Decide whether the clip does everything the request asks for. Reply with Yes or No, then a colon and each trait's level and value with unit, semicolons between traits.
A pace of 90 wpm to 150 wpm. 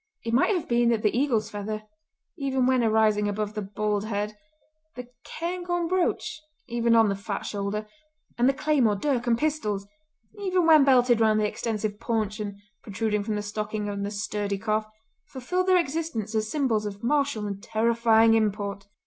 No: average, 175 wpm